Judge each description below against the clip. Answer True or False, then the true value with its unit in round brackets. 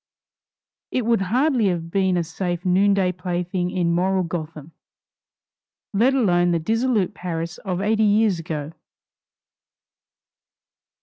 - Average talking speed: False (115 wpm)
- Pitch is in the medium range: True (180 Hz)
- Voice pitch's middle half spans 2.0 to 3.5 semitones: True (3.1 semitones)